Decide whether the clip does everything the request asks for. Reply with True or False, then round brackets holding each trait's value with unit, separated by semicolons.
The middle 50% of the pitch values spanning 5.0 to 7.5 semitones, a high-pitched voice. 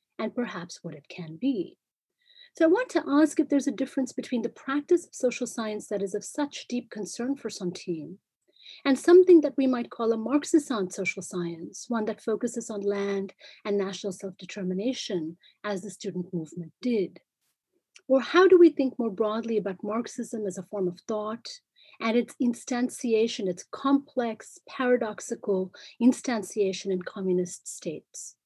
True (5.5 semitones; 225 Hz)